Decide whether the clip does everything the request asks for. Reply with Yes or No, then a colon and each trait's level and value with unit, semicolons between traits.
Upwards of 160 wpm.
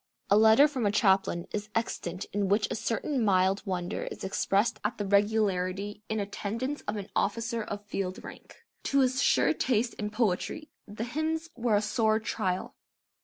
Yes: average, 170 wpm